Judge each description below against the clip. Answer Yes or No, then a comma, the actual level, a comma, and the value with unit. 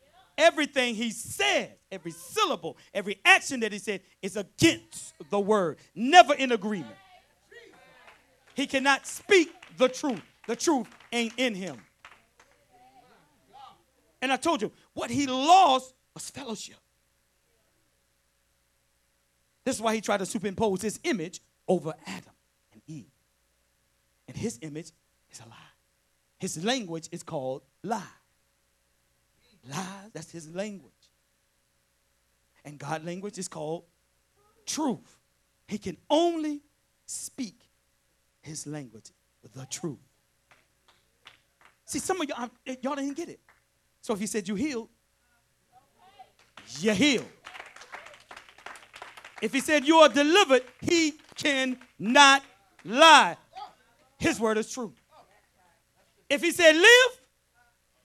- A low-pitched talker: No, high, 210 Hz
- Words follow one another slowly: Yes, slow, 115 wpm